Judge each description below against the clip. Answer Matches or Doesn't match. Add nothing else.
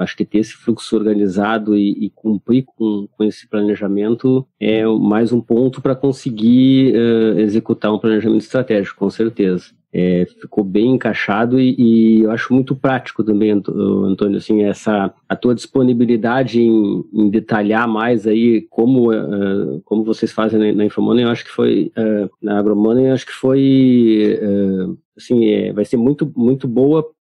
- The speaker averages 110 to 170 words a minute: Matches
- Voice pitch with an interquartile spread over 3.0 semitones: Doesn't match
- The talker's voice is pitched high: Doesn't match